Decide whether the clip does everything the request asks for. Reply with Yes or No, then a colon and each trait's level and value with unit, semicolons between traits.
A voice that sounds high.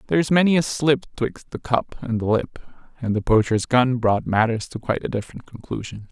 No: low, 125 Hz